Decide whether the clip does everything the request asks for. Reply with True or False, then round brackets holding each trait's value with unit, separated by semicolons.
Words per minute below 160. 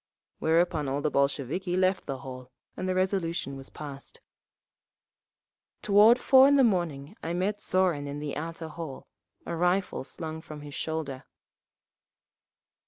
True (140 wpm)